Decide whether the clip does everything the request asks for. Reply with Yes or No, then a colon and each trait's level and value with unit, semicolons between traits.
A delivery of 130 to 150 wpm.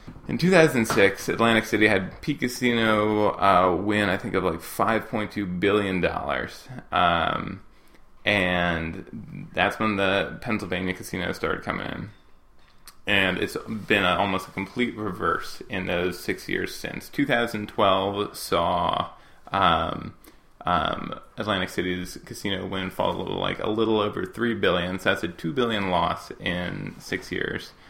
Yes: average, 140 wpm